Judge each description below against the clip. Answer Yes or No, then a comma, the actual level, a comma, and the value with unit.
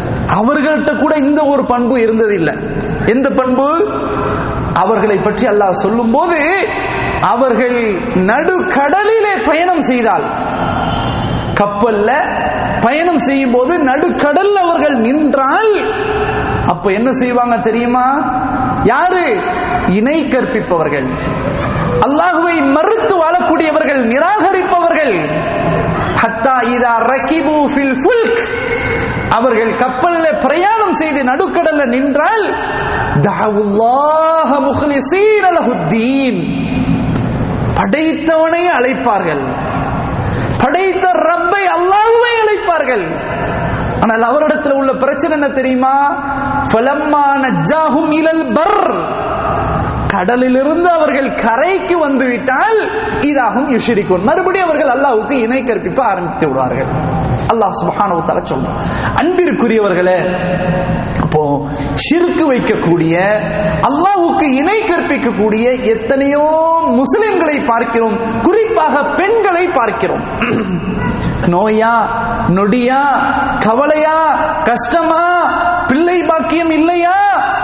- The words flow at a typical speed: No, slow, 75 wpm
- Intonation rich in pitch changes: Yes, wide, 6.3 semitones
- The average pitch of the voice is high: Yes, very high, 285 Hz